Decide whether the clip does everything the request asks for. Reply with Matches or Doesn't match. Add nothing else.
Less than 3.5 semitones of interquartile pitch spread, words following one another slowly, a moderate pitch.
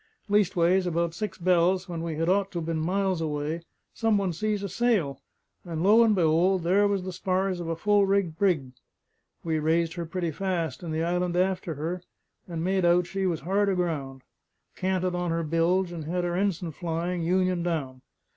Doesn't match